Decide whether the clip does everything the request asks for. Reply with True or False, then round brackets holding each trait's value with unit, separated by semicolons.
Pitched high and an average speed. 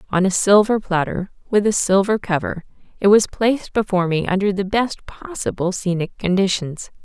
True (195 Hz; 160 wpm)